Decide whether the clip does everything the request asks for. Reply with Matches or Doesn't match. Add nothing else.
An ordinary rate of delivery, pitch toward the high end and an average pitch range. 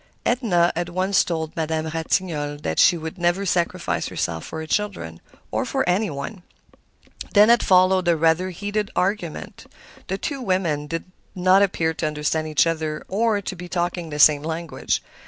Doesn't match